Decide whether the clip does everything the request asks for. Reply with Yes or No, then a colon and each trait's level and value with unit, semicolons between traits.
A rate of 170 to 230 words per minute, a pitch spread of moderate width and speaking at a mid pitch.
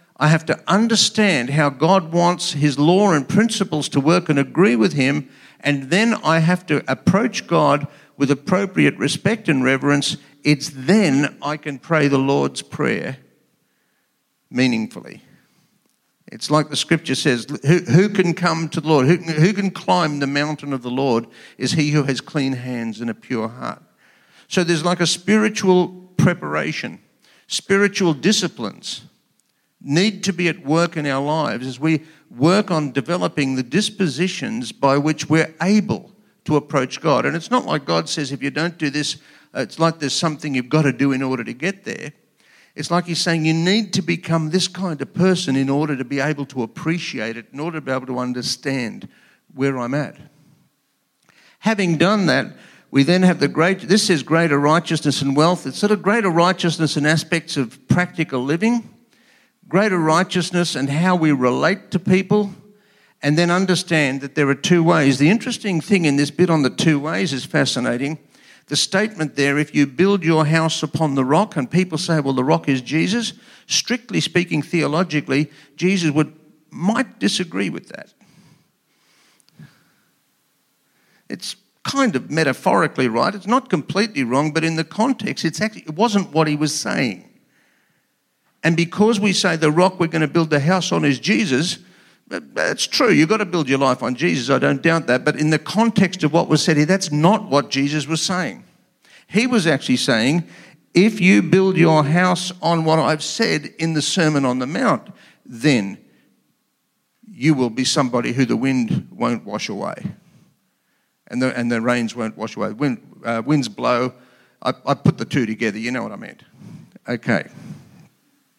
Yes: average, 180 wpm; average, 4.5 semitones; medium, 160 Hz